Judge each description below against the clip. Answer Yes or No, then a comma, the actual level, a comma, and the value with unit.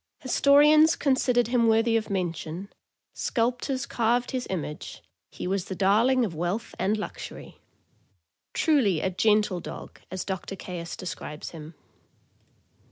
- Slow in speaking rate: Yes, slow, 125 wpm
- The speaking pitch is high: Yes, high, 210 Hz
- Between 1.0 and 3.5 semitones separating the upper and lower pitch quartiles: No, average, 5.2 semitones